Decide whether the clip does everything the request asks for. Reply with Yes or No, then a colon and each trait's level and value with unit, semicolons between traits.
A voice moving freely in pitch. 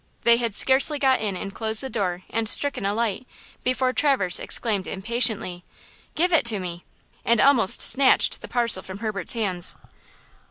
No: average, 4.6 semitones